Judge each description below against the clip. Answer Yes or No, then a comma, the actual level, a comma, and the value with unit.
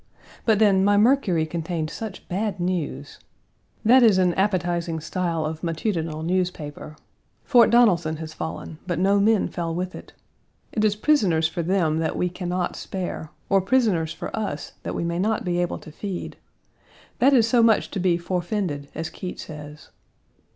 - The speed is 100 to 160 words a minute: No, average, 170 wpm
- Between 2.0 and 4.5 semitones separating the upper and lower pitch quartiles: Yes, average, 4.0 semitones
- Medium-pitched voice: Yes, medium, 180 Hz